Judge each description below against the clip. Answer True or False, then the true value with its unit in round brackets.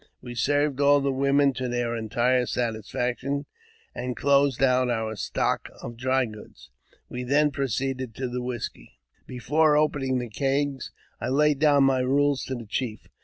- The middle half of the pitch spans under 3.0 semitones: True (2.5 semitones)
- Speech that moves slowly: False (160 wpm)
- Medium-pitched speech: False (130 Hz)